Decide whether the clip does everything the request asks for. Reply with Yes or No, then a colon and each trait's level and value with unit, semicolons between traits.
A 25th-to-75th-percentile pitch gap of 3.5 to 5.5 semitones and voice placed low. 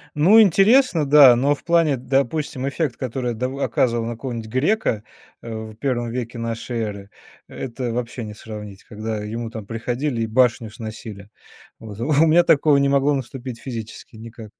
Yes: average, 3.8 semitones; low, 120 Hz